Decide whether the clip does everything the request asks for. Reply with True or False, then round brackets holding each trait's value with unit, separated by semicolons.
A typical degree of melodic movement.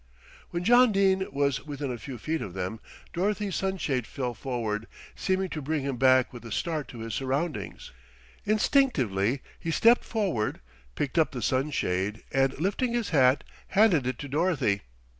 False (7.3 semitones)